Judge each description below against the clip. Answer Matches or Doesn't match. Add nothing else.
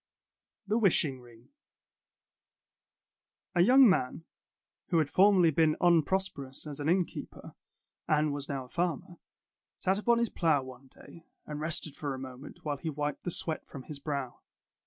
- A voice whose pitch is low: Doesn't match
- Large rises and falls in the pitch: Doesn't match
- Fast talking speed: Doesn't match